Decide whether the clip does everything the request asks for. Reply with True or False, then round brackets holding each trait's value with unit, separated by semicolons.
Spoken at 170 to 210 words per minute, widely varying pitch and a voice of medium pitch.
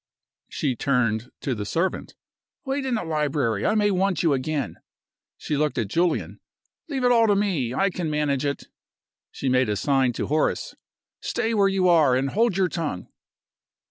True (175 wpm; 6.9 semitones; 155 Hz)